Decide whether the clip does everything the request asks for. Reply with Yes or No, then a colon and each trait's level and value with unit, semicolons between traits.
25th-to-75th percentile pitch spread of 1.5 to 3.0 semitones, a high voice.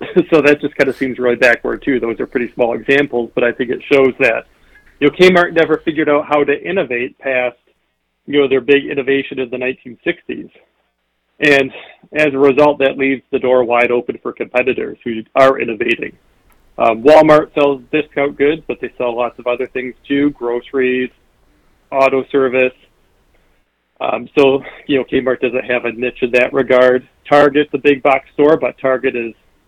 No: average, 2.7 semitones; low, 135 Hz